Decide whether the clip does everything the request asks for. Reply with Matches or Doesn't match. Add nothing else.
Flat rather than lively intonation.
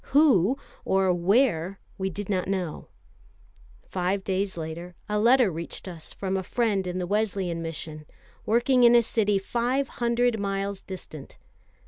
Doesn't match